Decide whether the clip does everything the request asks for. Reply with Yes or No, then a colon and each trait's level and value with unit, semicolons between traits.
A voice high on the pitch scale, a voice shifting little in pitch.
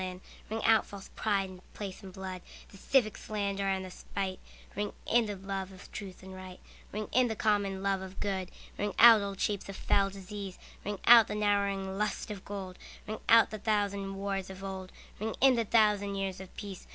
Yes: high, 200 Hz; narrow, 1.7 semitones